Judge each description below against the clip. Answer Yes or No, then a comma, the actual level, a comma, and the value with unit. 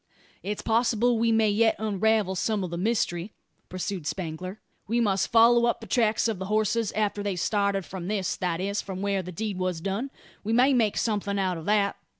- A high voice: Yes, high, 205 Hz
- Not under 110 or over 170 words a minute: No, average, 200 wpm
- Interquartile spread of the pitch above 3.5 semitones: No, average, 2.9 semitones